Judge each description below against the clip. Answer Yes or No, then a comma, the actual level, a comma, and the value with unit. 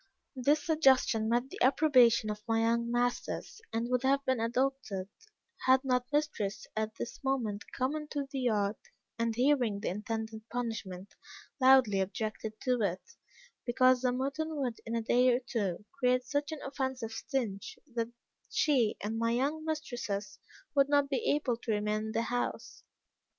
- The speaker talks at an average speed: Yes, average, 160 wpm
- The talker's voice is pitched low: No, high, 245 Hz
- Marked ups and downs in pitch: No, average, 3.5 semitones